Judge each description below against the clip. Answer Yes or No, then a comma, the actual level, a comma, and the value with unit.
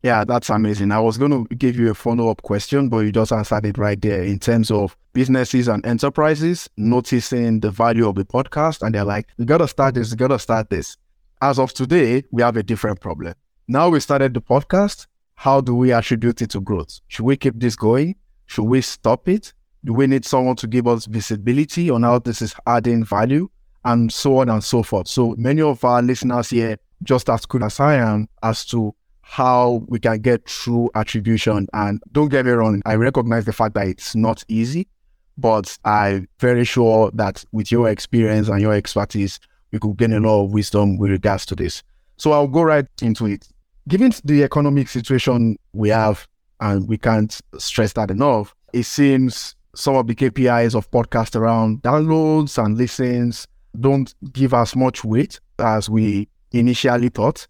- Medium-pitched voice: No, low, 115 Hz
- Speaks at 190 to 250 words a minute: Yes, average, 195 wpm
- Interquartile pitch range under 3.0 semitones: No, average, 3.3 semitones